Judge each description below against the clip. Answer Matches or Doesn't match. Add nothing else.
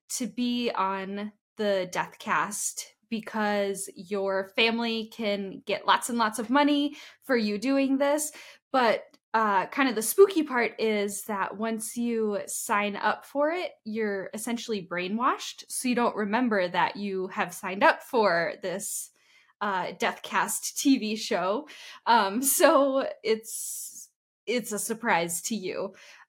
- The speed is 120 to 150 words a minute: Matches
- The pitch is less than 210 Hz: Doesn't match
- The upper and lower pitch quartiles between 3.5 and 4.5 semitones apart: Matches